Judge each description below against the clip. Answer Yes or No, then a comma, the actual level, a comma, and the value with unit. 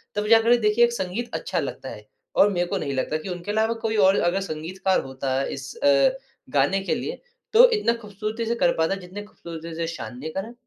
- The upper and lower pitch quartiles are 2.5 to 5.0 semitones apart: No, wide, 5.5 semitones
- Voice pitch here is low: No, high, 195 Hz